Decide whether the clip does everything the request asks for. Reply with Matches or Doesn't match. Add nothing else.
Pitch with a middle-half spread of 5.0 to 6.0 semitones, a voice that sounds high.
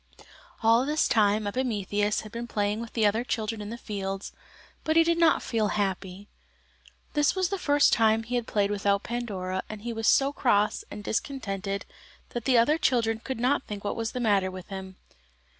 Doesn't match